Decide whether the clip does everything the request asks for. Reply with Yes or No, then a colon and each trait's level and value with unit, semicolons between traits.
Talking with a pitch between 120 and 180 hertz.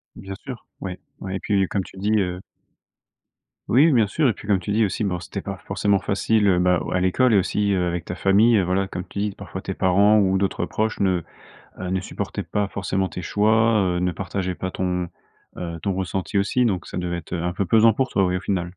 No: very low, 95 Hz